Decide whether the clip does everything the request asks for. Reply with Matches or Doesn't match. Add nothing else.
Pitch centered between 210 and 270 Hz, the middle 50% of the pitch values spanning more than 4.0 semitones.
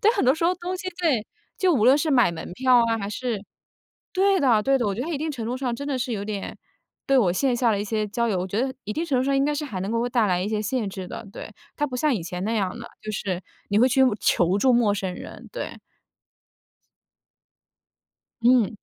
Matches